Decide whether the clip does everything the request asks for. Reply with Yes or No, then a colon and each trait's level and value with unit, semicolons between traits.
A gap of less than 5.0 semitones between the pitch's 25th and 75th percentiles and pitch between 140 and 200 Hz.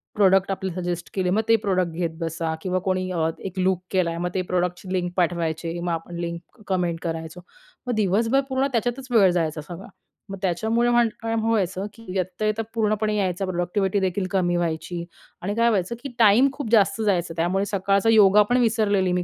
Yes: average, 3.4 semitones; high, 190 Hz